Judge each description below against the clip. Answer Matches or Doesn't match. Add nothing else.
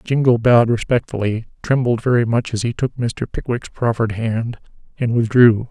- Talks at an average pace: Matches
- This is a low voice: Matches